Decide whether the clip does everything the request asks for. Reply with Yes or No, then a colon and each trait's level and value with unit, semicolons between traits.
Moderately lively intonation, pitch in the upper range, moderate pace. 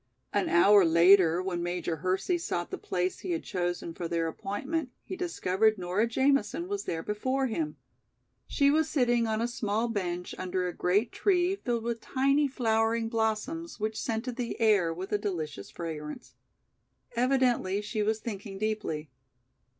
No: wide, 5.7 semitones; high, 215 Hz; average, 160 wpm